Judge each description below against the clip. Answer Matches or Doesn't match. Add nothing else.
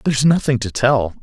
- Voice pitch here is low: Matches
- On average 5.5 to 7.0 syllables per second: Matches